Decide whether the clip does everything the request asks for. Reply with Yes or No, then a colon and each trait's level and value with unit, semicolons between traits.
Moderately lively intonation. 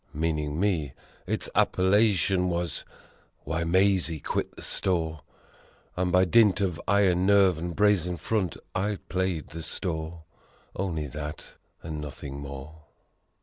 Yes: average, 3.3 semitones